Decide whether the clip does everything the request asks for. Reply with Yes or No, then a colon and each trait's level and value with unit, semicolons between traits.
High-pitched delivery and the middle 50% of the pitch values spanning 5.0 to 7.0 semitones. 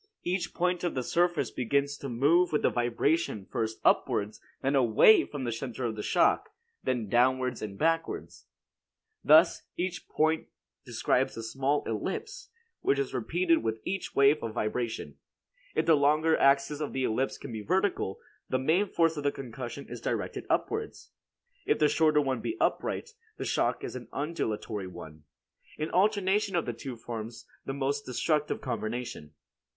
No: medium, 140 Hz; wide, 5.6 semitones